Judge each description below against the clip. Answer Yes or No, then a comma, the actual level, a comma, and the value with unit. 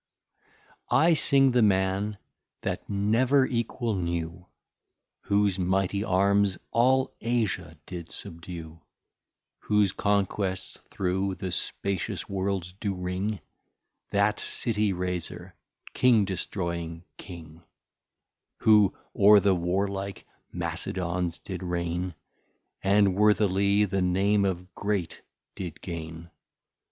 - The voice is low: Yes, very low, 95 Hz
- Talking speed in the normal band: No, slow, 100 wpm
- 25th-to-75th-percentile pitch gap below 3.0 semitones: Yes, narrow, 2.5 semitones